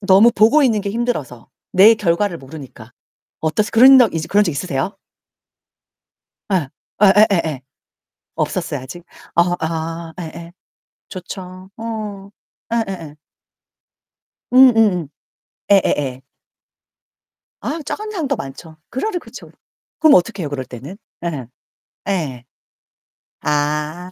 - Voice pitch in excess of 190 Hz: No, medium, 185 Hz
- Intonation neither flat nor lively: No, wide, 5.8 semitones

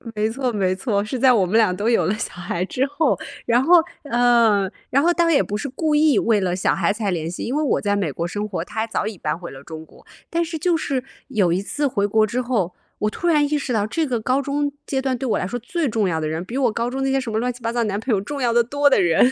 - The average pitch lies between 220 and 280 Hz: Yes, high, 230 Hz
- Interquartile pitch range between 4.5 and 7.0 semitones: Yes, average, 5.1 semitones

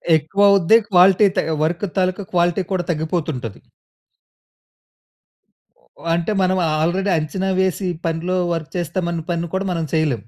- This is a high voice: No, medium, 175 Hz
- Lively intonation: No, average, 2.7 semitones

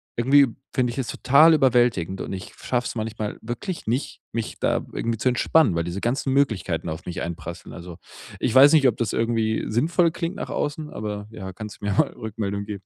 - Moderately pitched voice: No, low, 115 Hz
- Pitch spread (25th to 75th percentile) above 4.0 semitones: Yes, average, 4.9 semitones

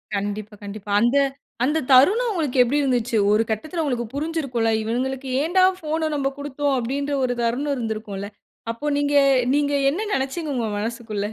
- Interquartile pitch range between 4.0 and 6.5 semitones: Yes, average, 4.4 semitones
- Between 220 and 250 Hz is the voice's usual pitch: No, very high, 265 Hz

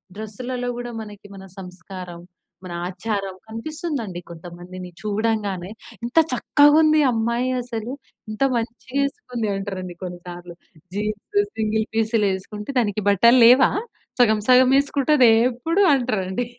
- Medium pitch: No, high, 220 Hz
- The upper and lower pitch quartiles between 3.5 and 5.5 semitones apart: Yes, average, 4.5 semitones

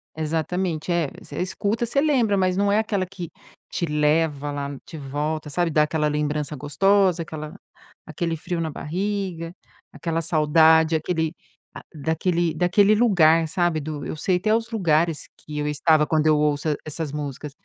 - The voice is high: No, medium, 160 Hz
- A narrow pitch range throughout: No, average, 3.1 semitones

